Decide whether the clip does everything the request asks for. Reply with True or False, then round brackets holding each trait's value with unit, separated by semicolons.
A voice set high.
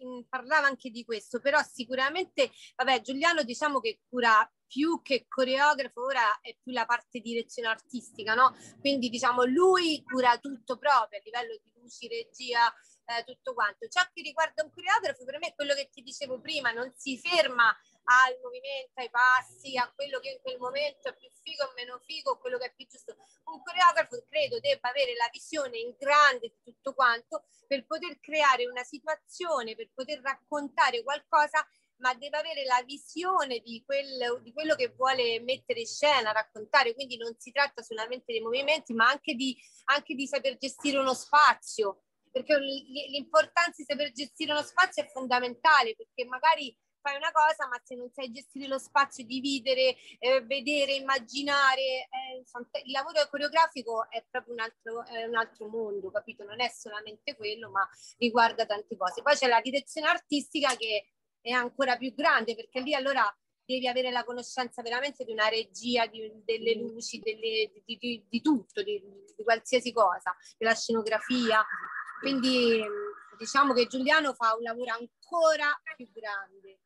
True (260 Hz)